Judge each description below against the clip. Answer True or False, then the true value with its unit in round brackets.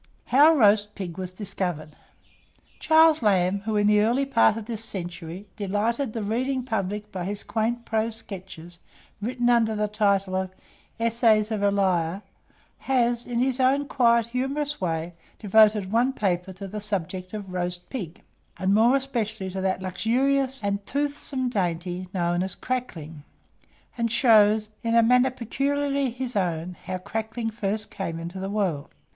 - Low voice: False (210 Hz)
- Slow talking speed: False (155 wpm)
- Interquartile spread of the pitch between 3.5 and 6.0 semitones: True (4.3 semitones)